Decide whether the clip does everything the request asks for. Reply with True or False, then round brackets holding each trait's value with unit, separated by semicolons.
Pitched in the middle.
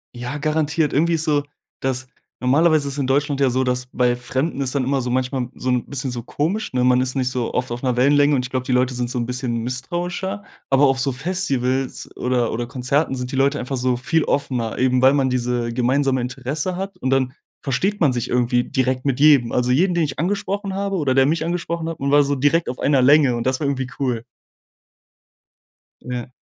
False (130 Hz)